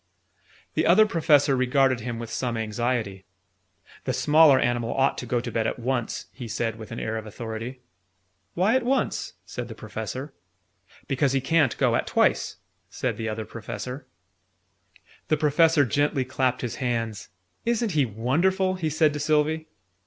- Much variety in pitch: No, average, 4.8 semitones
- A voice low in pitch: Yes, low, 130 Hz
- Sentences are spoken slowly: No, average, 160 wpm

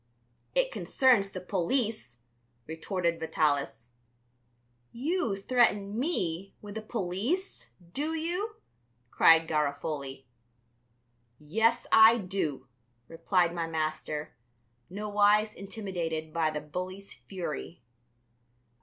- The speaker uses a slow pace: Yes, slow, 90 wpm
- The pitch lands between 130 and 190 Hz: Yes, medium, 185 Hz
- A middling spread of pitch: No, wide, 5.7 semitones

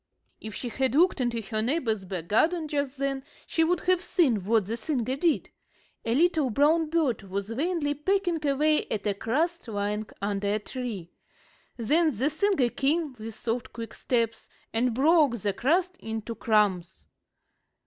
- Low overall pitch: No, very high, 255 Hz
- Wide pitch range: Yes, wide, 6.3 semitones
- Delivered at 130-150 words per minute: No, average, 160 wpm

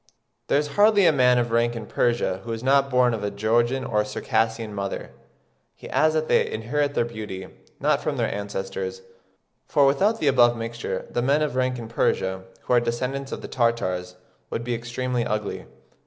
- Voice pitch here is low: Yes, low, 120 Hz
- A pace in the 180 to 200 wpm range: Yes, average, 190 wpm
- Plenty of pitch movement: No, average, 3.5 semitones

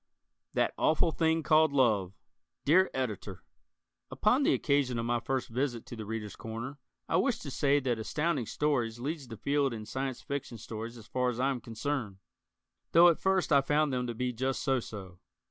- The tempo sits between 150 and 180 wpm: No, average, 190 wpm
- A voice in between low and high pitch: No, low, 130 Hz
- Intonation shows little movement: No, average, 4.1 semitones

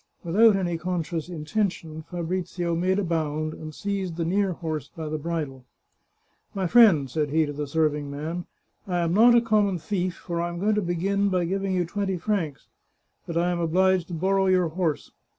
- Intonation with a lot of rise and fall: No, average, 3.1 semitones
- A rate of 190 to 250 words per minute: Yes, fast, 205 wpm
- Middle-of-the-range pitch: Yes, medium, 175 Hz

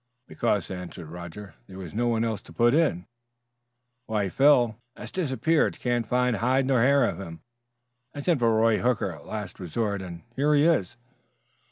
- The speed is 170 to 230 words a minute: Yes, average, 185 wpm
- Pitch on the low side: Yes, low, 115 Hz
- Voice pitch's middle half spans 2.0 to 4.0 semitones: No, average, 5.1 semitones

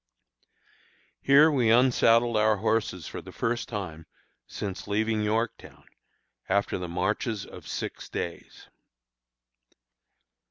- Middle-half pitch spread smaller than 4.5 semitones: Yes, average, 2.9 semitones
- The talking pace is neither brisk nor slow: No, slow, 105 wpm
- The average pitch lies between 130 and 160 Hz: No, low, 110 Hz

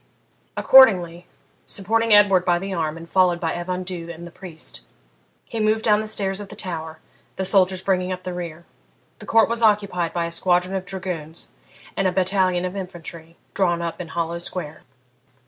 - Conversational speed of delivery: Yes, average, 180 wpm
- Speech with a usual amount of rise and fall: No, narrow, 2.2 semitones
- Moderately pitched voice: Yes, medium, 180 Hz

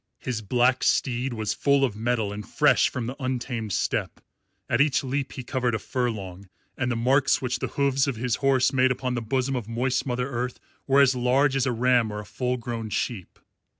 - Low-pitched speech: Yes, low, 125 Hz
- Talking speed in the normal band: No, fast, 210 wpm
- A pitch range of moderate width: No, narrow, 2.2 semitones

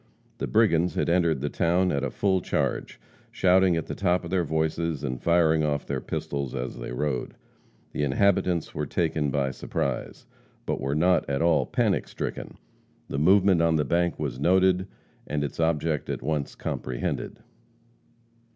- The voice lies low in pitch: Yes, very low, 80 Hz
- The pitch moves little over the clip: No, average, 3.7 semitones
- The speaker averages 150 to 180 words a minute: Yes, average, 165 wpm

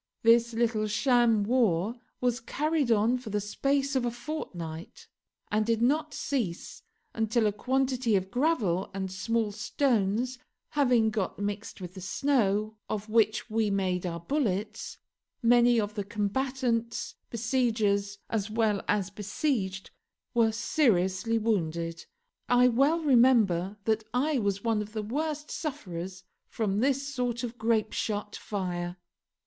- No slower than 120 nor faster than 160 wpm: Yes, slow, 135 wpm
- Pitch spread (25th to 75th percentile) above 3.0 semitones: Yes, average, 3.7 semitones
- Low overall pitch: No, high, 225 Hz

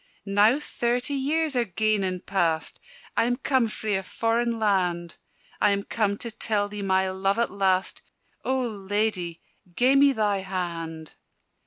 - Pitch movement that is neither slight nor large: Yes, average, 3.8 semitones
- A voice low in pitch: No, high, 205 Hz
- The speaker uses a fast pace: No, average, 155 wpm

